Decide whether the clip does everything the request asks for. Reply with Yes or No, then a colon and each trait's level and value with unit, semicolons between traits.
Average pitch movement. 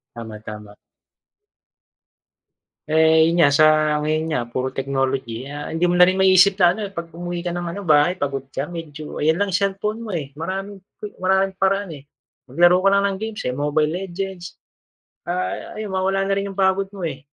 Yes: average, 4.6 semitones